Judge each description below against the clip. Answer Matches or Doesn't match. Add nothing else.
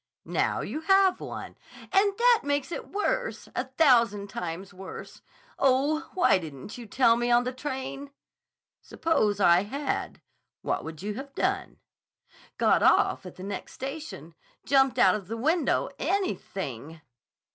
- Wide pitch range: Matches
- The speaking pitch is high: Matches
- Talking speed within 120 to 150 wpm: Matches